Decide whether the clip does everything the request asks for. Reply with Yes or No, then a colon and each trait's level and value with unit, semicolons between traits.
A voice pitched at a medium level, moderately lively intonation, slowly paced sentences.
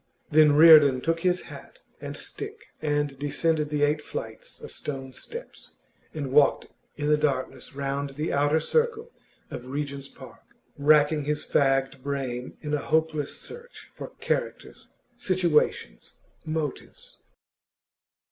No: medium, 150 Hz; narrow, 2.3 semitones; slow, 130 wpm